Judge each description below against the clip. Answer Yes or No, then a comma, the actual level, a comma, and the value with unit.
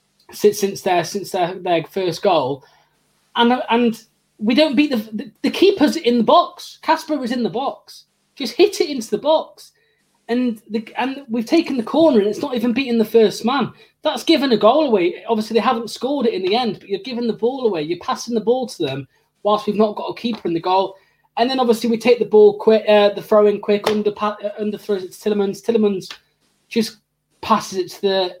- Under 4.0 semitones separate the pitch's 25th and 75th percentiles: Yes, average, 3.6 semitones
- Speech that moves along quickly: Yes, fast, 220 wpm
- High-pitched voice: Yes, high, 225 Hz